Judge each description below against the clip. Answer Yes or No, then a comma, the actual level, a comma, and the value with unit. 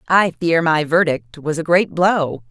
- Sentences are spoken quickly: No, average, 190 wpm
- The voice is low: No, medium, 160 Hz